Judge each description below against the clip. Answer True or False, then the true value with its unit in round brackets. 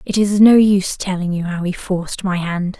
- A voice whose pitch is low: False (185 Hz)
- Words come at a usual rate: False (235 wpm)